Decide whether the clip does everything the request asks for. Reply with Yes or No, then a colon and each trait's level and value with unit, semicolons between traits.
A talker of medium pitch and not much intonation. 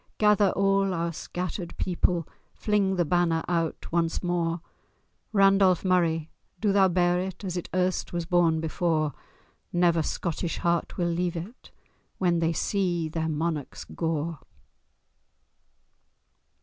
Yes: medium, 175 Hz; narrow, 2.0 semitones